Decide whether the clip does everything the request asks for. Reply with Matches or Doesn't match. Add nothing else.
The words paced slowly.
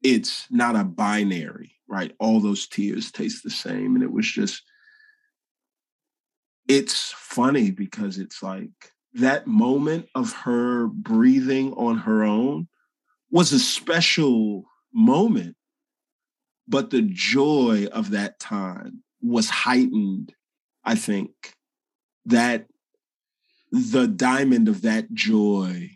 Matches